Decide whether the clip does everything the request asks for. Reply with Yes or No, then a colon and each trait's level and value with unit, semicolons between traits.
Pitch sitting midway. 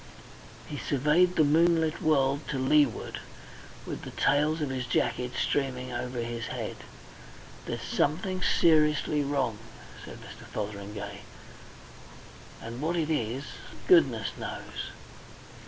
Yes: medium, 145 Hz